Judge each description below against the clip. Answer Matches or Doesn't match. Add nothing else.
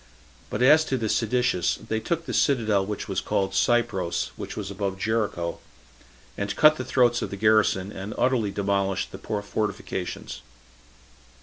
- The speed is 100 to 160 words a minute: Matches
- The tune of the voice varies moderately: Matches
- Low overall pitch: Matches